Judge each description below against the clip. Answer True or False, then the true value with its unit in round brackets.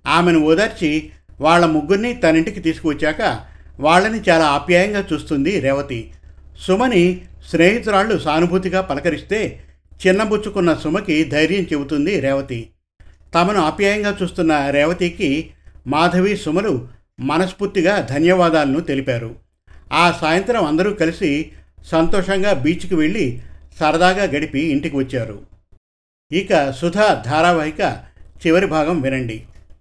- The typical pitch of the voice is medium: True (160 Hz)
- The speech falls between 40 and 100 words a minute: True (95 wpm)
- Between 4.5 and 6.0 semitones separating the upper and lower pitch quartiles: True (5.5 semitones)